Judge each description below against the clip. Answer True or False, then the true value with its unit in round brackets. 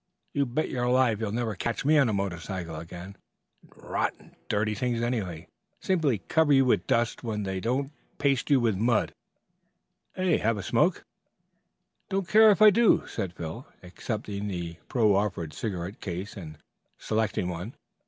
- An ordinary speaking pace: True (160 wpm)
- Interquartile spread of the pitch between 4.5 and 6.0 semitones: True (5.4 semitones)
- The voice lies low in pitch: True (110 Hz)